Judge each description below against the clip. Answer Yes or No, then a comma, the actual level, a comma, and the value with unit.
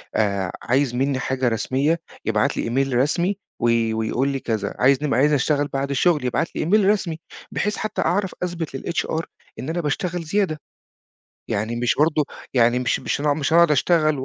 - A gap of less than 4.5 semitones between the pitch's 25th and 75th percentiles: No, average, 4.9 semitones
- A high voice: No, medium, 140 Hz